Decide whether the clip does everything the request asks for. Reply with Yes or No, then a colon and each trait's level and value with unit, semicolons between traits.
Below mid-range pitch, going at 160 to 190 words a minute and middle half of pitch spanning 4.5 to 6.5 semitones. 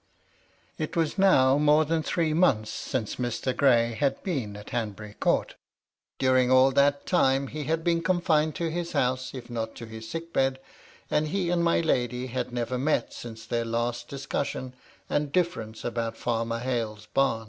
Yes: low, 130 Hz; average, 175 wpm; average, 4.9 semitones